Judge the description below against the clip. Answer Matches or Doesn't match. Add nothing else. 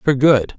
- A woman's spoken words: Doesn't match